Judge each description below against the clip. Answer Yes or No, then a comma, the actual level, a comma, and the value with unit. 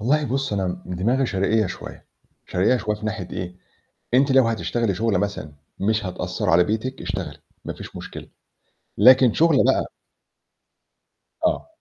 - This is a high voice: No, low, 110 Hz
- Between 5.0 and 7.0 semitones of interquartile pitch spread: Yes, wide, 5.4 semitones